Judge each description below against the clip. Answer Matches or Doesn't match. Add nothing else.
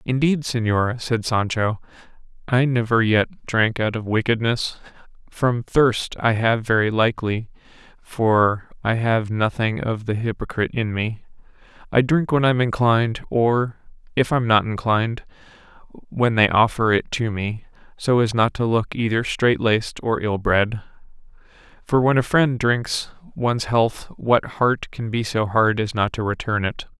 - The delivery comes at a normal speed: Matches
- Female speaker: Doesn't match